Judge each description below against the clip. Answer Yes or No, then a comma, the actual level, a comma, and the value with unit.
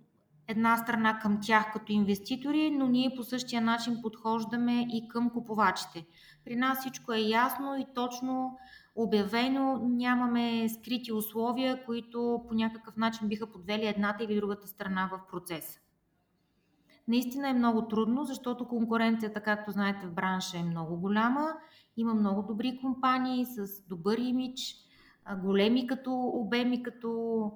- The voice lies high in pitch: Yes, high, 230 Hz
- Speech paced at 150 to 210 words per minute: No, average, 135 wpm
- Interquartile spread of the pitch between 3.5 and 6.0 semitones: No, average, 2.9 semitones